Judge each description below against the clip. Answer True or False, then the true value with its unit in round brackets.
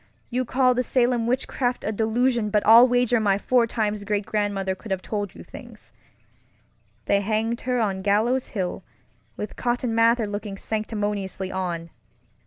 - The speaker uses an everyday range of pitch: True (3.1 semitones)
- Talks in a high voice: True (215 Hz)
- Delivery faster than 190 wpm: False (155 wpm)